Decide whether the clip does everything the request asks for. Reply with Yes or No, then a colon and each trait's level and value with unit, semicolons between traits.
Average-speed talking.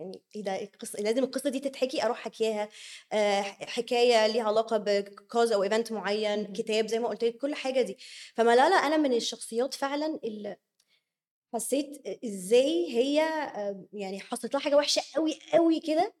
No: fast, 150 wpm